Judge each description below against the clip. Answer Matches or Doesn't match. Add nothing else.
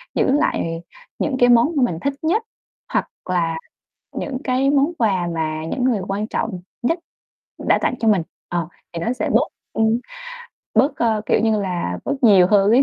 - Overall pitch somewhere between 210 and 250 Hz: Matches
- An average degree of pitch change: Doesn't match